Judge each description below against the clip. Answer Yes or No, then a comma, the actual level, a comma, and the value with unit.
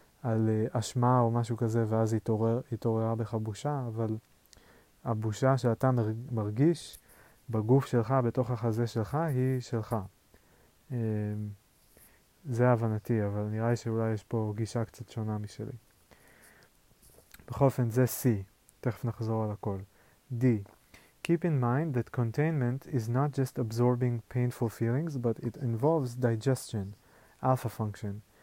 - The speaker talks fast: No, average, 130 wpm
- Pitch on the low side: Yes, low, 115 Hz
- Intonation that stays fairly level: Yes, narrow, 2.3 semitones